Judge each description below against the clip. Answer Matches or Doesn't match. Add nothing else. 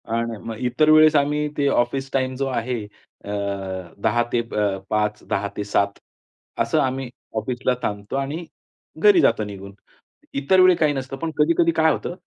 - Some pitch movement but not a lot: Doesn't match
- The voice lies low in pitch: Matches